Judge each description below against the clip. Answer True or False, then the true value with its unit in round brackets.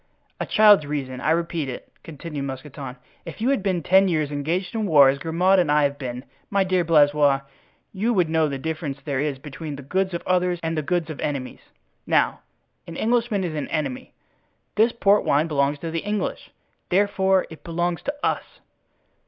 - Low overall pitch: False (160 Hz)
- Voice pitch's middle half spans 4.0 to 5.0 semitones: True (4.6 semitones)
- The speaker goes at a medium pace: True (185 wpm)